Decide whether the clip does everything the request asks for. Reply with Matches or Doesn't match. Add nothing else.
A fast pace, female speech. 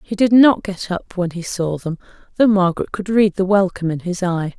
Matches